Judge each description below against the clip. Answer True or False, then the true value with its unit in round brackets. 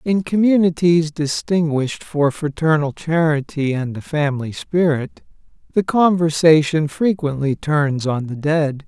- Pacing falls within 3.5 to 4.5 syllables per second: True (4.2 syllables/s)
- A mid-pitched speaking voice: True (155 Hz)